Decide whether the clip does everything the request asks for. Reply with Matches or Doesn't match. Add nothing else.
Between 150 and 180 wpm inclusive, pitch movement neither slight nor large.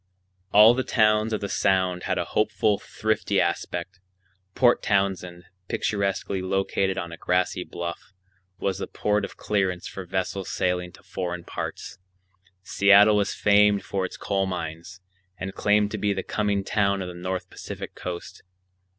Doesn't match